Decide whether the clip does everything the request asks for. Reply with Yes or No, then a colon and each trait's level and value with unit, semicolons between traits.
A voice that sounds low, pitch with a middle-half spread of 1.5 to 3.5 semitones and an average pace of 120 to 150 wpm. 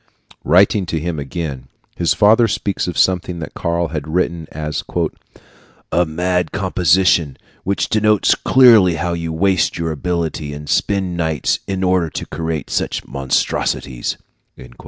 Yes: very low, 85 Hz; average, 2.9 semitones; slow, 135 wpm